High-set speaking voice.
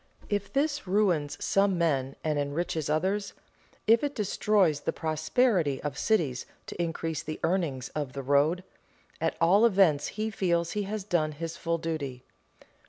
No: medium, 165 Hz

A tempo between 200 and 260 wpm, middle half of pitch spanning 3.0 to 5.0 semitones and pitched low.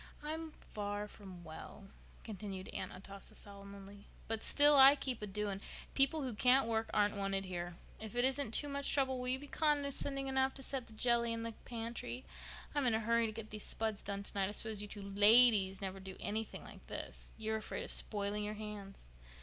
No: fast, 205 wpm; average, 4.1 semitones; high, 220 Hz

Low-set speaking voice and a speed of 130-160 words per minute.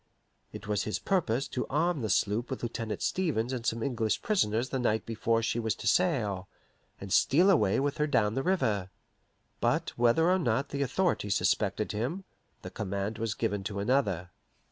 No: low, 115 Hz; average, 180 wpm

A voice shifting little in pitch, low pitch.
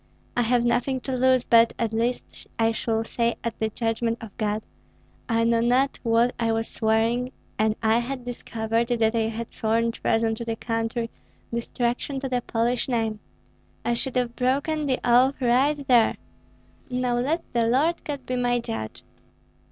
No: narrow, 1.7 semitones; high, 235 Hz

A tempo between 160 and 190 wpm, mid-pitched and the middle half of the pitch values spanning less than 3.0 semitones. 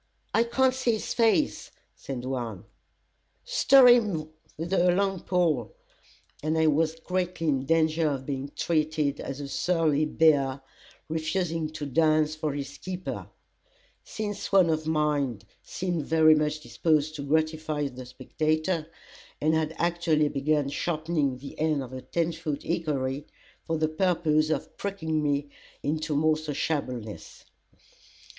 No: slow, 135 wpm; medium, 155 Hz; narrow, 2.6 semitones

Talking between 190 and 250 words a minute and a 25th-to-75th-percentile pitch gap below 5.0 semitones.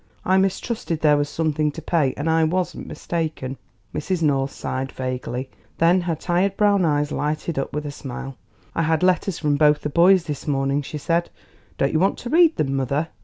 Yes: average, 195 wpm; average, 3.5 semitones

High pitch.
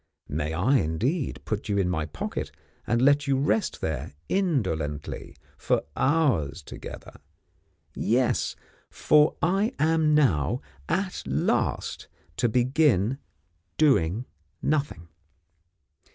No: low, 125 Hz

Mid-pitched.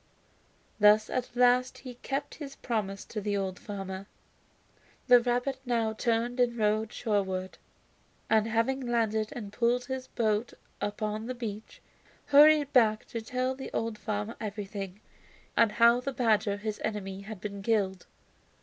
No: high, 220 Hz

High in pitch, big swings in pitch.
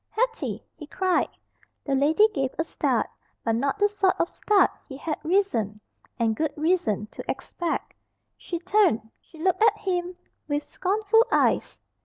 Yes: very high, 340 Hz; wide, 6.3 semitones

